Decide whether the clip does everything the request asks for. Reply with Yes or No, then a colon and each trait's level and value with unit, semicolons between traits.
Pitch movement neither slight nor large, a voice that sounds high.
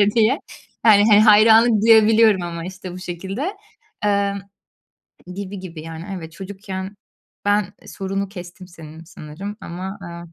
Yes: average, 3.0 semitones; high, 195 Hz